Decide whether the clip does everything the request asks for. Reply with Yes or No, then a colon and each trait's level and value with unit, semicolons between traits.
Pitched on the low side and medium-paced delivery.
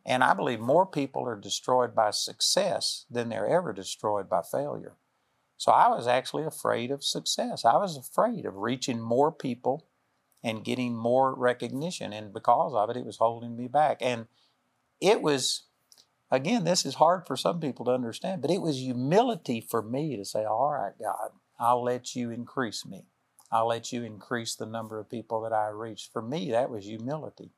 Yes: low, 120 Hz; average, 185 wpm